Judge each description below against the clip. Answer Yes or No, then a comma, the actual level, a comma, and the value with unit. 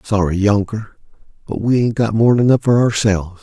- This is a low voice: Yes, low, 110 Hz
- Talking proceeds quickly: No, average, 175 wpm